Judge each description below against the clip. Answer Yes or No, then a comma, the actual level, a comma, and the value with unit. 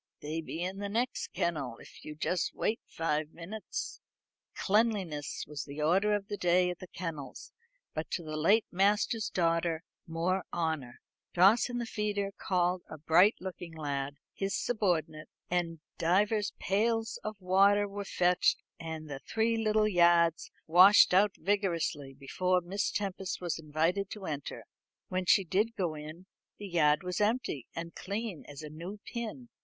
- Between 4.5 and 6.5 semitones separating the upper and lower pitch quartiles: No, average, 4.1 semitones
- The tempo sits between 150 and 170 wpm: Yes, average, 160 wpm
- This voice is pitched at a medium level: Yes, medium, 180 Hz